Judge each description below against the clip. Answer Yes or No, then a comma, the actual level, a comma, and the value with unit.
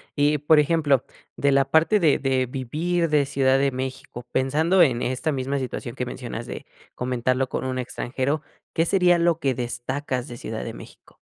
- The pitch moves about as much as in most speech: Yes, average, 3.4 semitones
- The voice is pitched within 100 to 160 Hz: Yes, low, 135 Hz